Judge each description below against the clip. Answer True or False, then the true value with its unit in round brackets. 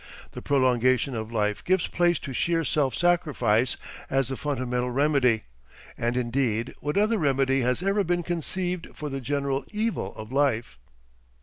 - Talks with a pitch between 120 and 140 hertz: True (135 Hz)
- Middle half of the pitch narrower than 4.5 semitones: False (5.1 semitones)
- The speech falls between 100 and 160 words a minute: True (150 wpm)